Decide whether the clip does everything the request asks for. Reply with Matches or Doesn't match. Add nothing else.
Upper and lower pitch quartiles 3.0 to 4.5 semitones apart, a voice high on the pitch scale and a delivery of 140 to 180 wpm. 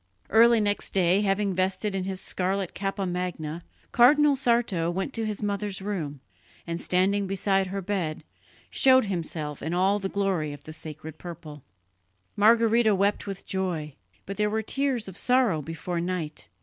Matches